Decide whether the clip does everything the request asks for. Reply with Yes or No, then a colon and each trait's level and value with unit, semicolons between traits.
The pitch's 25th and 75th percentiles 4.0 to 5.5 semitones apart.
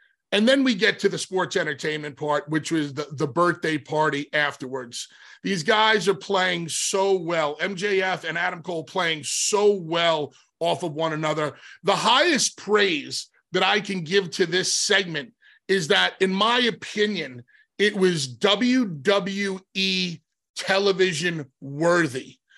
Yes: average, 4.5 semitones